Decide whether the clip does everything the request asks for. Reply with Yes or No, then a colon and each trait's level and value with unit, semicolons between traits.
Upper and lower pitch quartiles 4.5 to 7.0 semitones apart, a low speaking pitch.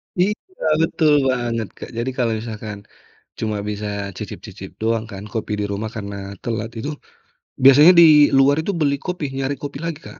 Yes: average, 5.0 semitones; low, 120 Hz